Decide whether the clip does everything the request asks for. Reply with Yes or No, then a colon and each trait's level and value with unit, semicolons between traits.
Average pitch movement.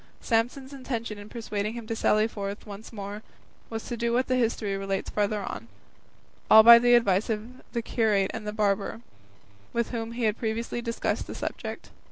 No: narrow, 2.2 semitones